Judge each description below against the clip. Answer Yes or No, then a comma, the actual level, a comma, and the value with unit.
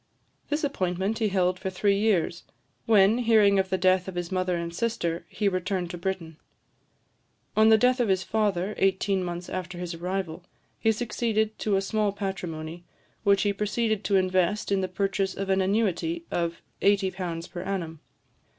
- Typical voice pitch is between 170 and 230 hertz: Yes, high, 190 Hz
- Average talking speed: Yes, average, 170 wpm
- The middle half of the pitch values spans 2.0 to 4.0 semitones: Yes, average, 2.8 semitones